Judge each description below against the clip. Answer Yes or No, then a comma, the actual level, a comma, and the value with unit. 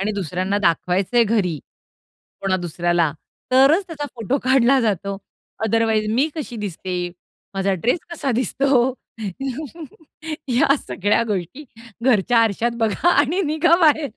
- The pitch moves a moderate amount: No, wide, 6.1 semitones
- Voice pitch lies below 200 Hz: No, high, 230 Hz